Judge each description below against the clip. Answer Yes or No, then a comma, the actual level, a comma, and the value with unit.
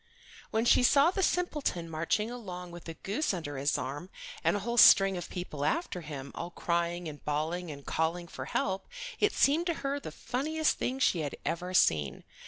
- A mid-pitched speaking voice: Yes, medium, 180 Hz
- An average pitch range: No, wide, 7.6 semitones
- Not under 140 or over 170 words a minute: No, average, 190 wpm